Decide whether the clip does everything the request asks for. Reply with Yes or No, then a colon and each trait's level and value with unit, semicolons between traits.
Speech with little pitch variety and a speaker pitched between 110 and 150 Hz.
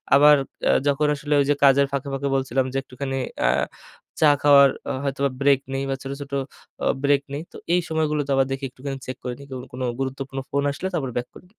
Yes: narrow, 1.1 semitones; medium, 140 Hz